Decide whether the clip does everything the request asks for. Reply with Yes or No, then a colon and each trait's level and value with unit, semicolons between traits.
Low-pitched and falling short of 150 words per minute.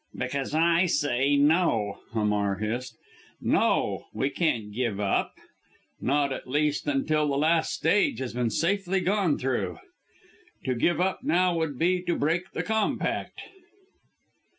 No: medium, 145 Hz; slow, 135 wpm